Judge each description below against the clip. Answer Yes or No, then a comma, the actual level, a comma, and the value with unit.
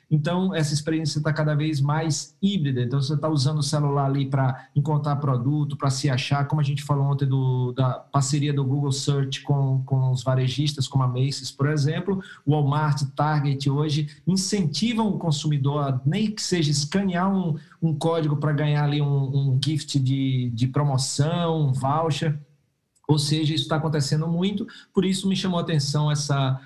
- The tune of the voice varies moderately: No, narrow, 2.1 semitones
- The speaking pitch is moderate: Yes, medium, 145 Hz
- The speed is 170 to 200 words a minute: Yes, average, 180 wpm